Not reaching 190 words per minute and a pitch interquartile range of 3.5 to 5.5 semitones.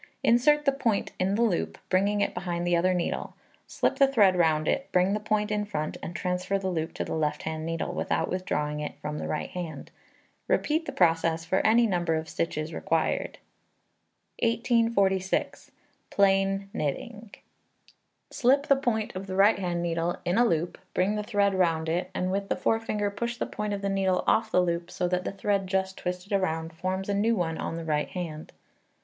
No: average, 195 wpm; average, 3.9 semitones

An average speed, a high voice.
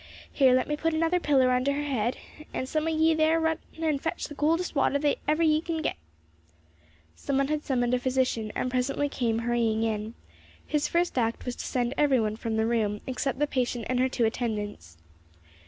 No: fast, 210 wpm; very high, 260 Hz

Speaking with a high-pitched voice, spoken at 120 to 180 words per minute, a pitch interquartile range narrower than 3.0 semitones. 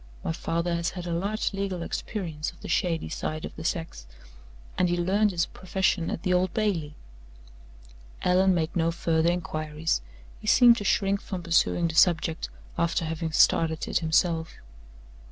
No: medium, 170 Hz; average, 165 wpm; narrow, 2.4 semitones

